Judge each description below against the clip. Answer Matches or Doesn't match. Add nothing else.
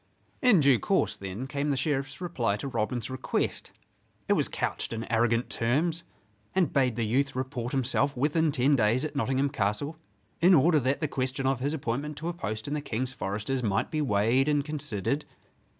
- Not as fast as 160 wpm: Doesn't match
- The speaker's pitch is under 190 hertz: Matches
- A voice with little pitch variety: Doesn't match